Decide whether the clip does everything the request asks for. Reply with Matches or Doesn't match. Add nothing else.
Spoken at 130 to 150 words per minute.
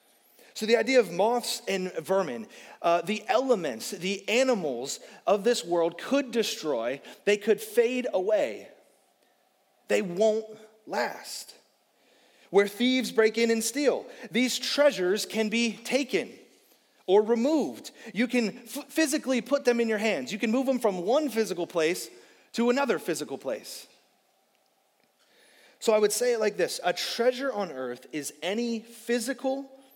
Matches